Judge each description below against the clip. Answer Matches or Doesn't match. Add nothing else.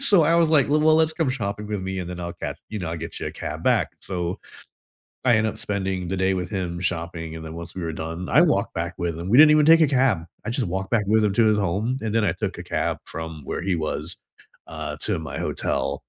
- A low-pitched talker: Matches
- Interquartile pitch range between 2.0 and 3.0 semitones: Doesn't match